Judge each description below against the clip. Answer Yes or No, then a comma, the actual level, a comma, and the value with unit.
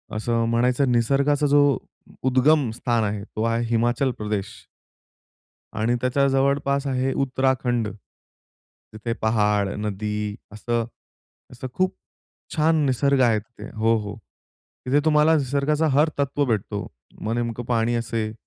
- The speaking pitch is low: Yes, low, 120 Hz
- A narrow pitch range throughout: No, average, 3.9 semitones